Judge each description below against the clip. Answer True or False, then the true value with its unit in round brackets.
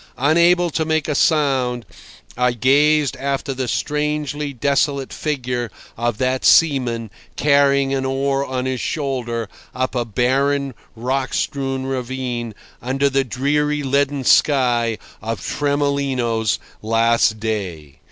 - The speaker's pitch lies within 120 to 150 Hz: True (135 Hz)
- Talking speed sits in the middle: False (120 wpm)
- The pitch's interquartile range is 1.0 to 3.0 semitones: True (2.7 semitones)